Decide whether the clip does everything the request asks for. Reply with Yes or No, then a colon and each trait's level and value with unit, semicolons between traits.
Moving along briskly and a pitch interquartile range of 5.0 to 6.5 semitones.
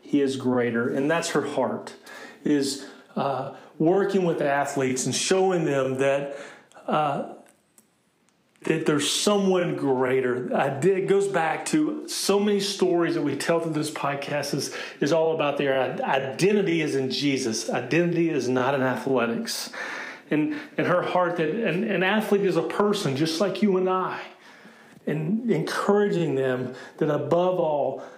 No: average, 155 wpm; wide, 5.5 semitones